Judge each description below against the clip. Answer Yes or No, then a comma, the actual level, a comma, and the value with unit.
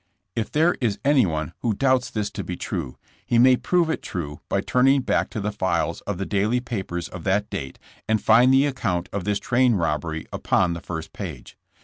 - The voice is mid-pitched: No, low, 105 Hz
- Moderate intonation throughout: No, wide, 6.3 semitones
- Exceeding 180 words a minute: Yes, fast, 205 wpm